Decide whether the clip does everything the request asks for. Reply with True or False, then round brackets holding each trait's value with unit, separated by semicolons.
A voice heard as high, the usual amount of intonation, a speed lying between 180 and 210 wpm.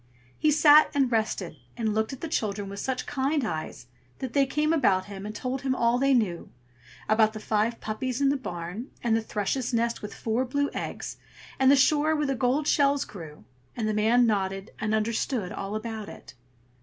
True (230 Hz; 4.2 semitones; 200 wpm)